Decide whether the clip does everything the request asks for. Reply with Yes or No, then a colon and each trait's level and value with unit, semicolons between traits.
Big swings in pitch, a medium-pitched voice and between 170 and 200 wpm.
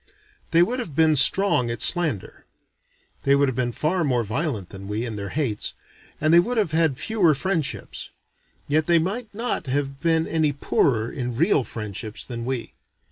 Yes: wide, 5.7 semitones; medium, 145 Hz; average, 180 wpm